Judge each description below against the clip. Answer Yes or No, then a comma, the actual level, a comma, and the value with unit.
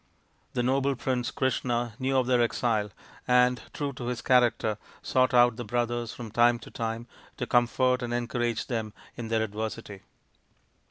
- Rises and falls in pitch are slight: Yes, narrow, 1.6 semitones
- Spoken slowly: No, average, 160 wpm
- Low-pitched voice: Yes, low, 120 Hz